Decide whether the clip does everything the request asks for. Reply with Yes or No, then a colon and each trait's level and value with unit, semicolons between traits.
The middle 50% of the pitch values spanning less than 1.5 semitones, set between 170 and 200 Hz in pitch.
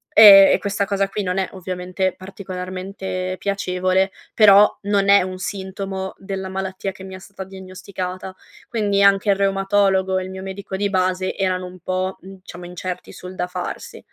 Yes: narrow, 1.1 semitones; high, 190 Hz